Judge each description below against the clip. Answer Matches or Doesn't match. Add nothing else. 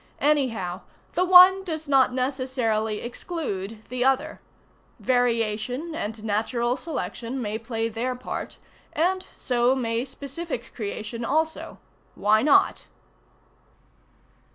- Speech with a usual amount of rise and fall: Matches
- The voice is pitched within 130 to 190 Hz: Doesn't match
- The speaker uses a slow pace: Matches